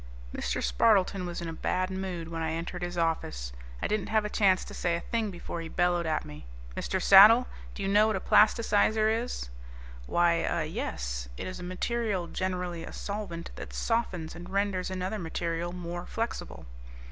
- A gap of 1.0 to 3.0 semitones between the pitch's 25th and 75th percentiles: No, average, 3.4 semitones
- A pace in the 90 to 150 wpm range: No, average, 185 wpm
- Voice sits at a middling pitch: Yes, medium, 180 Hz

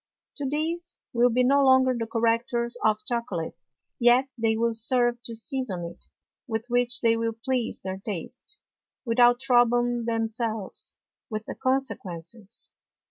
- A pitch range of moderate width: No, narrow, 2.0 semitones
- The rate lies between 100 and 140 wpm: Yes, slow, 135 wpm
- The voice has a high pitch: Yes, high, 235 Hz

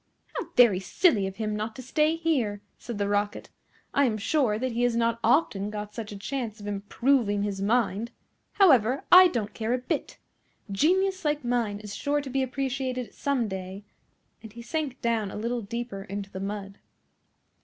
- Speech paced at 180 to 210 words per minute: Yes, average, 185 wpm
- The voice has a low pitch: No, high, 230 Hz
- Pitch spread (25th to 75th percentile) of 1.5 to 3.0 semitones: No, average, 4.4 semitones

